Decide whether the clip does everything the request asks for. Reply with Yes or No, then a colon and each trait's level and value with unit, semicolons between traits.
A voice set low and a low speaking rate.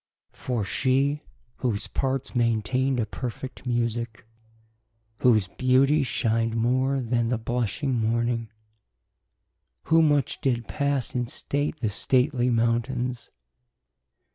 Yes: low, 125 Hz; slow, 105 wpm